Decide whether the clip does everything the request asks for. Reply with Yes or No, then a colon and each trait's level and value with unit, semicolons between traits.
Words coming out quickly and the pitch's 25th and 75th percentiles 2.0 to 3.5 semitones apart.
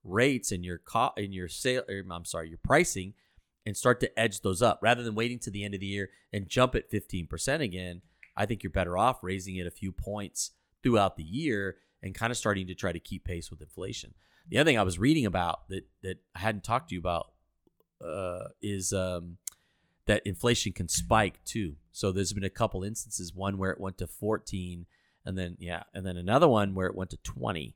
Yes: fast, 225 wpm; average, 3.1 semitones